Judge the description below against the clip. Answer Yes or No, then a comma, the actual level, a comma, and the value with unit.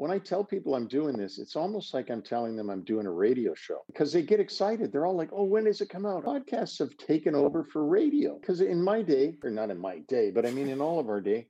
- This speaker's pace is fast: Yes, fast, 280 wpm